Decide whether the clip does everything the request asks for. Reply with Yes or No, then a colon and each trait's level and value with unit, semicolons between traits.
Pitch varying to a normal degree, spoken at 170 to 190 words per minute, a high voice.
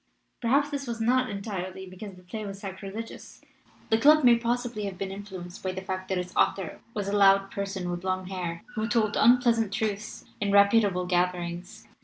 Yes: average, 3.3 semitones; average, 185 wpm; high, 200 Hz